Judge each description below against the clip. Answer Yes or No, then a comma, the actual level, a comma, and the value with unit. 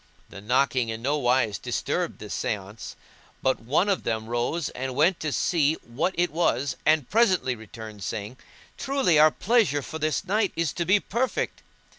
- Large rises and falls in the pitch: Yes, wide, 6.8 semitones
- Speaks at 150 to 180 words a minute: Yes, average, 170 wpm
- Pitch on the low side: No, medium, 145 Hz